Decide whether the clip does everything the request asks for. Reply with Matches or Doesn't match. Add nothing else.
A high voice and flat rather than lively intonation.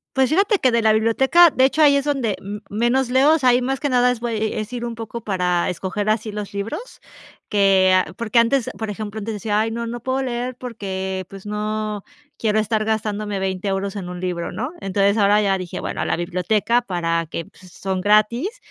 Doesn't match